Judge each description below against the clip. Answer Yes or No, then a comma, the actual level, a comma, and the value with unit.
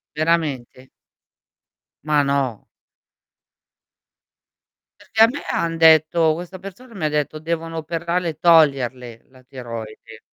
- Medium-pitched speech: Yes, medium, 155 Hz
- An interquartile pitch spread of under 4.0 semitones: No, average, 4.4 semitones